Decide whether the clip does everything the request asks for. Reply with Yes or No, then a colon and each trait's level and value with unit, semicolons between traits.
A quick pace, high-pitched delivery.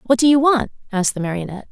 Yes: fast, 245 wpm; high, 225 Hz